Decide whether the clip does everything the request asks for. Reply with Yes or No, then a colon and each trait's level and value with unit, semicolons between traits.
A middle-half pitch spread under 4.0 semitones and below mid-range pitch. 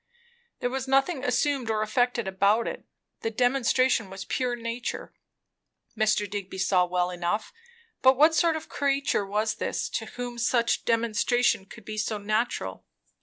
No: average, 3.6 semitones; high, 235 Hz